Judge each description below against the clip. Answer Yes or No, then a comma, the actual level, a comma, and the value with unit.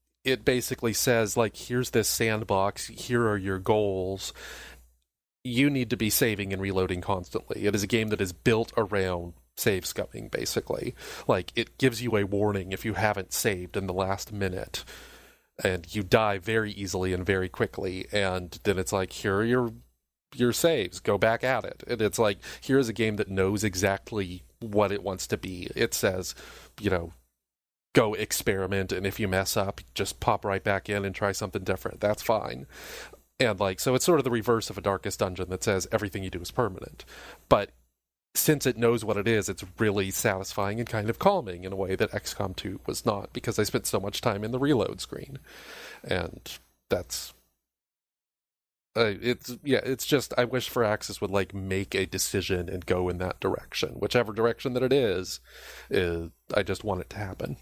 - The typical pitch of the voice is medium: No, low, 100 Hz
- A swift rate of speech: No, average, 195 wpm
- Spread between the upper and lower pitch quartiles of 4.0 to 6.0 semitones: No, average, 3.5 semitones